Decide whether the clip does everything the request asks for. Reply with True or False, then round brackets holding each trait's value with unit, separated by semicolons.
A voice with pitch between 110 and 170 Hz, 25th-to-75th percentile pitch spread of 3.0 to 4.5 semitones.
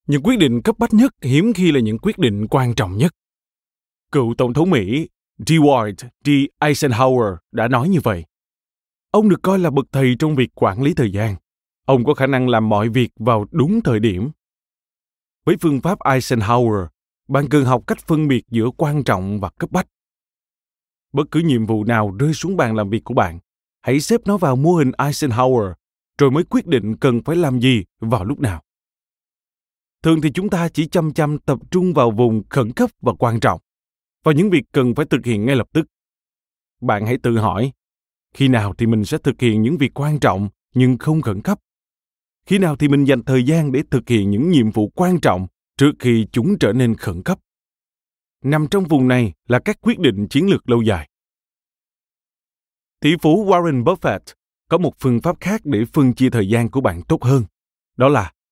False (135 Hz; 5.2 semitones)